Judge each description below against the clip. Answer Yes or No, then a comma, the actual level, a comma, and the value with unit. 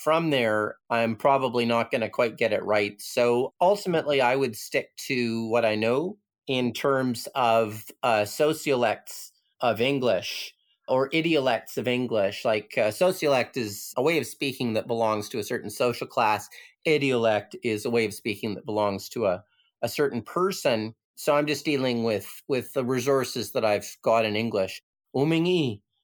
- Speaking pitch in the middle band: No, low, 120 Hz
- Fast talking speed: No, average, 170 wpm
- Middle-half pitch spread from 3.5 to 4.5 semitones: Yes, average, 4.1 semitones